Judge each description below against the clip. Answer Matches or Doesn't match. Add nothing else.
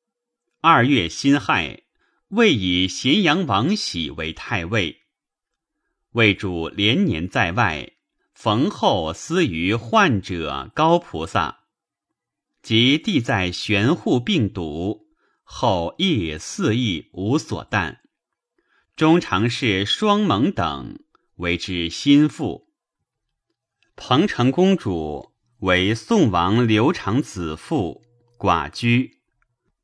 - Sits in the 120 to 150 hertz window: Doesn't match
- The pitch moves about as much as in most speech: Doesn't match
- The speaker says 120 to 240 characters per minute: Matches